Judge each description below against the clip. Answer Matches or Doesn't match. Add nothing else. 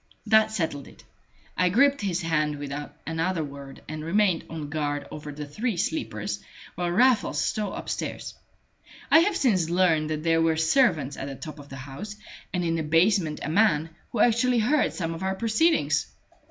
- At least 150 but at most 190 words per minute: Matches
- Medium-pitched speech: Matches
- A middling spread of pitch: Doesn't match